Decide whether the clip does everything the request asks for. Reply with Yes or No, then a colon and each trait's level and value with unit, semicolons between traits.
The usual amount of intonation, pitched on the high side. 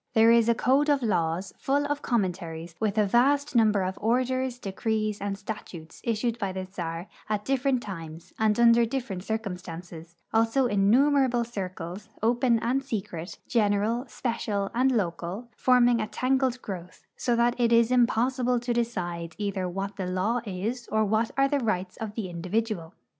Yes: average, 4.4 semitones; high, 220 Hz